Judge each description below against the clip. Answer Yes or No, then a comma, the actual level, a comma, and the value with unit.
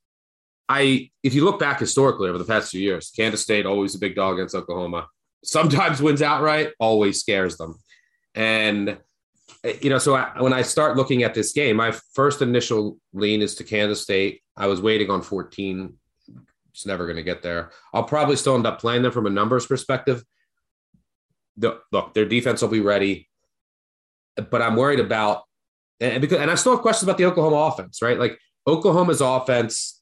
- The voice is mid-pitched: No, low, 115 Hz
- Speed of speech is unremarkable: Yes, average, 185 wpm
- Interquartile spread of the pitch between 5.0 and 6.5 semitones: Yes, average, 5.3 semitones